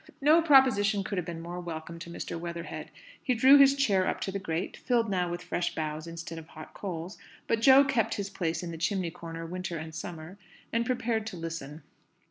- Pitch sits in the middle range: Yes, medium, 180 Hz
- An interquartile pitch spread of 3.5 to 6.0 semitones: Yes, average, 5.2 semitones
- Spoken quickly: Yes, fast, 210 wpm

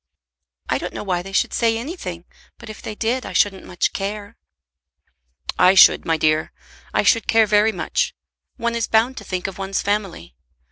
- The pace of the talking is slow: No, average, 185 wpm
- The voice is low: No, high, 205 Hz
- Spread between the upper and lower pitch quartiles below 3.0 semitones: No, average, 3.6 semitones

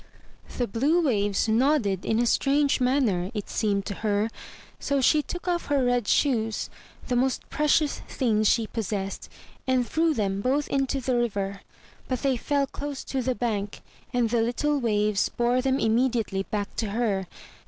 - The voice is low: No, high, 240 Hz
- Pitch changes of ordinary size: Yes, average, 4.4 semitones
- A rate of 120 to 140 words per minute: No, average, 165 wpm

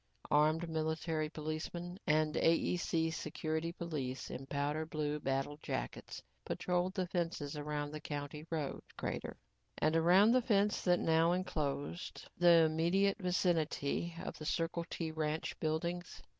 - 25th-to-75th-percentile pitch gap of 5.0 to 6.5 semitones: No, narrow, 2.4 semitones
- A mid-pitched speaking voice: Yes, medium, 160 Hz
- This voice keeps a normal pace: No, slow, 130 wpm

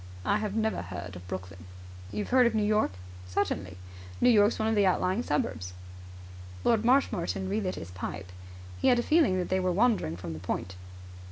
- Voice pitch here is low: No, medium, 185 Hz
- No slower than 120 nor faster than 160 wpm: No, average, 185 wpm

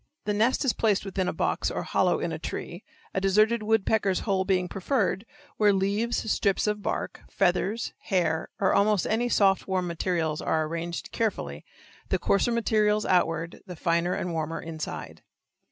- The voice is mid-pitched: No, high, 195 Hz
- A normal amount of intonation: Yes, average, 3.5 semitones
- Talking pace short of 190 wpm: Yes, average, 165 wpm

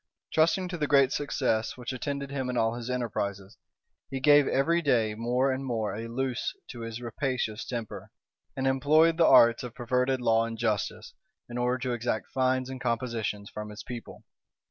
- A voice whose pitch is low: Yes, low, 125 Hz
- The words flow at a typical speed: Yes, average, 180 wpm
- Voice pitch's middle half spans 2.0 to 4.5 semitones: Yes, average, 2.7 semitones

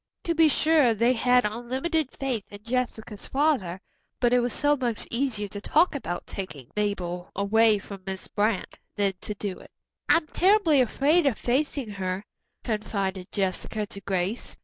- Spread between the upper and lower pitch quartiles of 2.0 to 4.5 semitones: No, average, 5.2 semitones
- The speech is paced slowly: No, average, 160 wpm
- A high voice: Yes, high, 225 Hz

